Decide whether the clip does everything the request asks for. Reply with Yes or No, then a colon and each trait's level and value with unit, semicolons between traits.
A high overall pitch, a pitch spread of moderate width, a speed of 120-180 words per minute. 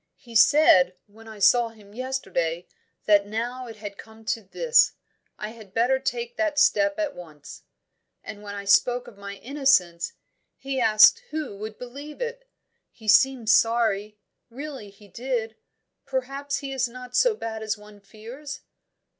Yes: high, 230 Hz; average, 4.6 semitones; average, 155 wpm